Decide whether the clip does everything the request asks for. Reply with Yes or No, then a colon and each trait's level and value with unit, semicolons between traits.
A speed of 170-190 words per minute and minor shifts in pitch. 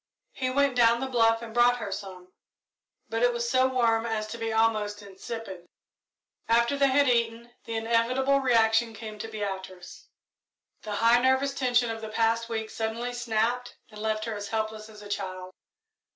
Yes: average, 175 wpm; narrow, 2.0 semitones